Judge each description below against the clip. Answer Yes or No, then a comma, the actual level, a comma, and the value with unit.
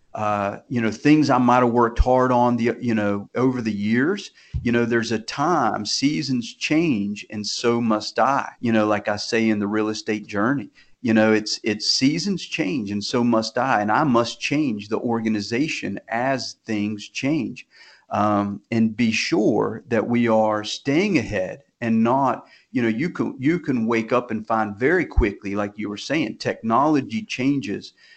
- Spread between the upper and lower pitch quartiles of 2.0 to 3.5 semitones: Yes, average, 2.7 semitones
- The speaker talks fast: No, average, 180 wpm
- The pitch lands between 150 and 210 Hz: No, low, 115 Hz